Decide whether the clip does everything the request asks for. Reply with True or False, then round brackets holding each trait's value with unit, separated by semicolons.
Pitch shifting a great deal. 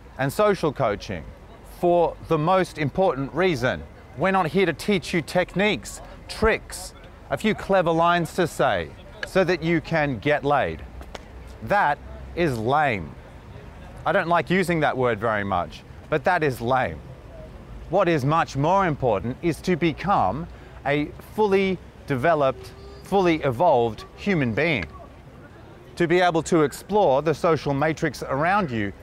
True (6.6 semitones)